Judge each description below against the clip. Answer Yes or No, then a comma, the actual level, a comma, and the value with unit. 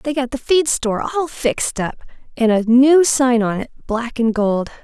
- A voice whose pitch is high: Yes, very high, 250 Hz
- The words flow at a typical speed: No, fast, 210 wpm